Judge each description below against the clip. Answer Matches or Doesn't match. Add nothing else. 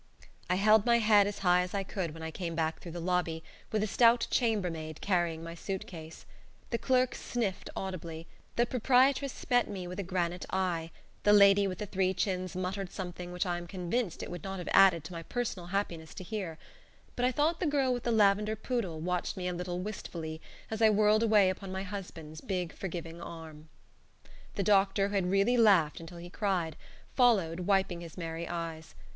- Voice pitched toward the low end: Doesn't match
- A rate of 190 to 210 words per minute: Matches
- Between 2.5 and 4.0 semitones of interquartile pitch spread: Matches